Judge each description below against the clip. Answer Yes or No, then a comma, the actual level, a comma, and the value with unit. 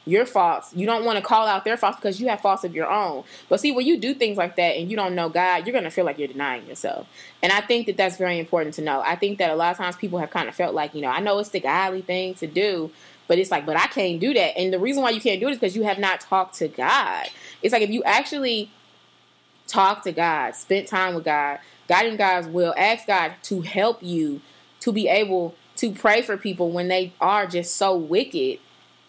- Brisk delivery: Yes, fast, 265 wpm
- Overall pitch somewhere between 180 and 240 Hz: Yes, high, 190 Hz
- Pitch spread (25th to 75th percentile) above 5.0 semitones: No, average, 3.7 semitones